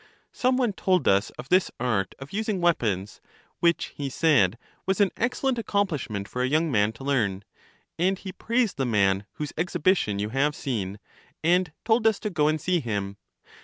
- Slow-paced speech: No, average, 185 wpm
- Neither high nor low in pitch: Yes, medium, 150 Hz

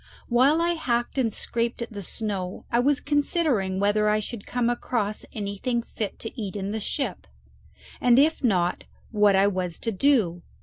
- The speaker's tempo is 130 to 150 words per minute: No, average, 175 wpm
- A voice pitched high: Yes, high, 225 Hz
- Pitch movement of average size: Yes, average, 3.8 semitones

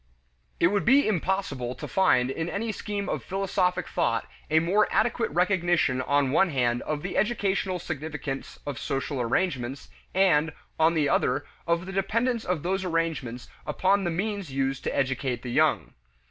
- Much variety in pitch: Yes, wide, 5.9 semitones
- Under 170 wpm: Yes, average, 160 wpm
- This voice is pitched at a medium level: Yes, medium, 170 Hz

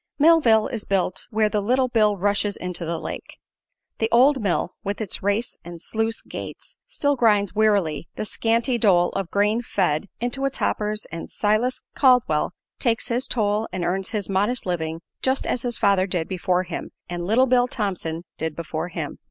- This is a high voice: Yes, high, 205 Hz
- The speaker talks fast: No, average, 175 wpm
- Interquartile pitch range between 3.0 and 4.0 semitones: No, average, 4.6 semitones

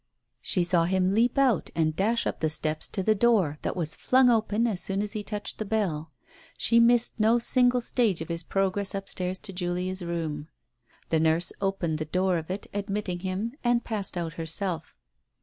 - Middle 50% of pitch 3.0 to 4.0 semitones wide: No, average, 4.4 semitones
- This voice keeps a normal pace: Yes, average, 190 wpm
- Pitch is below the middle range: No, high, 190 Hz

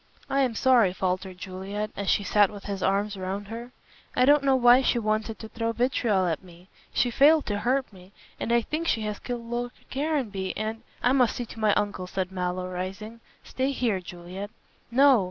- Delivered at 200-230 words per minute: Yes, fast, 205 wpm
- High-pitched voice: Yes, high, 215 Hz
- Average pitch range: Yes, average, 4.3 semitones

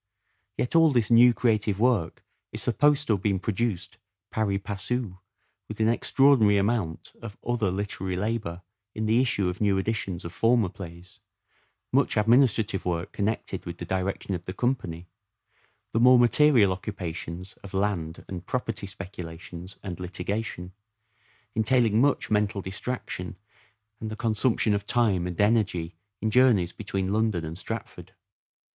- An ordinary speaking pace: Yes, average, 145 wpm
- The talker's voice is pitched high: No, low, 105 Hz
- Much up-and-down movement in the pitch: No, average, 3.8 semitones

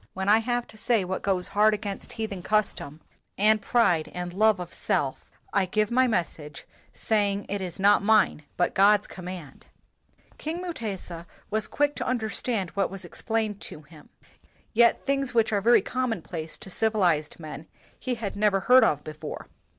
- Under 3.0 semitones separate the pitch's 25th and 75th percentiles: No, average, 3.8 semitones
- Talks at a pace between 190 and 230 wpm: No, average, 165 wpm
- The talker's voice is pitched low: No, high, 205 Hz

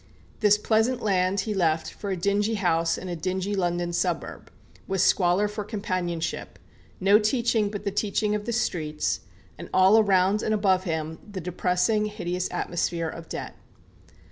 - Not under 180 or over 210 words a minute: No, average, 160 wpm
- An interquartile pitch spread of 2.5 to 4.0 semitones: Yes, average, 3.1 semitones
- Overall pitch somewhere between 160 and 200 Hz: Yes, high, 190 Hz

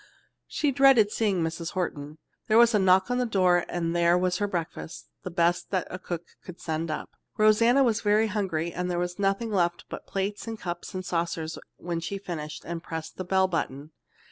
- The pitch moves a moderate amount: Yes, average, 3.5 semitones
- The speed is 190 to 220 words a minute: Yes, average, 195 wpm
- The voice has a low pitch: No, medium, 180 Hz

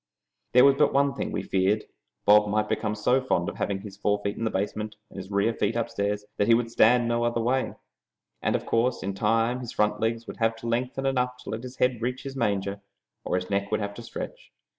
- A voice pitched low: Yes, low, 115 Hz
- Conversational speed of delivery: No, fast, 235 wpm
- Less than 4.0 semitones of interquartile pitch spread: Yes, average, 3.1 semitones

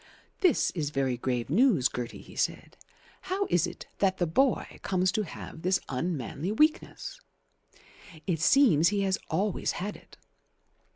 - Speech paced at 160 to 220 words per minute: No, average, 150 wpm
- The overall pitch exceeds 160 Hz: Yes, medium, 185 Hz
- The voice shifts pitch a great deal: Yes, wide, 6.0 semitones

